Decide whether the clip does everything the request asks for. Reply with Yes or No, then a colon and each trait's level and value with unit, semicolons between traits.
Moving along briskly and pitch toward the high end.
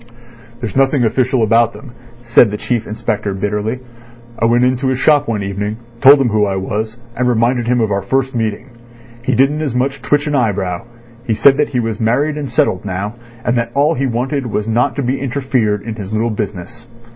No: fast, 210 wpm; low, 120 Hz